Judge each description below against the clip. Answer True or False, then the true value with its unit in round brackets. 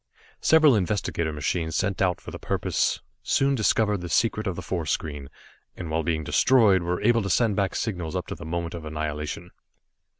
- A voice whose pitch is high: False (90 Hz)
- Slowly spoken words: False (190 wpm)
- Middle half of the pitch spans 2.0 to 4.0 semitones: False (4.6 semitones)